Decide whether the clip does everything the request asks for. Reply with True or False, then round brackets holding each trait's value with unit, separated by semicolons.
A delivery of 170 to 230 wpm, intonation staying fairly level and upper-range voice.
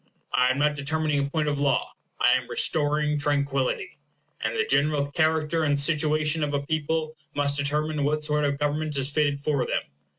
False (185 wpm; 1.5 semitones; 150 Hz)